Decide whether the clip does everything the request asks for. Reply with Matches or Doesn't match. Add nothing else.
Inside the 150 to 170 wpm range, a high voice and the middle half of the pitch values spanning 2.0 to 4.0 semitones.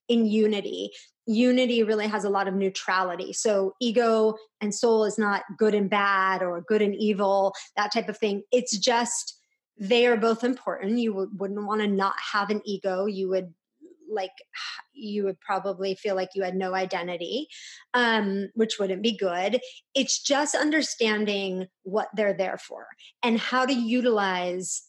Matches